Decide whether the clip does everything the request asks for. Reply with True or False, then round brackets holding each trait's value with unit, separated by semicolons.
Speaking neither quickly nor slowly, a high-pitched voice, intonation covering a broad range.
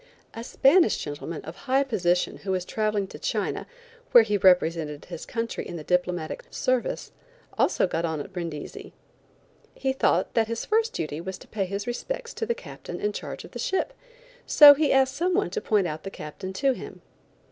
True (190 wpm; 210 Hz; 7.2 semitones)